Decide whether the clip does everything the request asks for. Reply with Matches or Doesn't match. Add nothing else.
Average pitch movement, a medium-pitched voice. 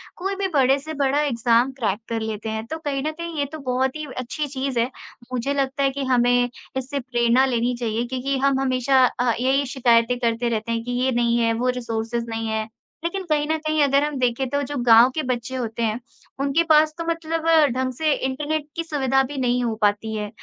Doesn't match